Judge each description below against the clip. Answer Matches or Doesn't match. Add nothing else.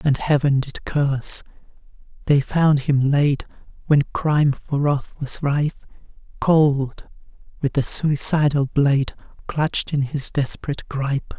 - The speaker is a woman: Matches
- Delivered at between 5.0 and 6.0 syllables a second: Doesn't match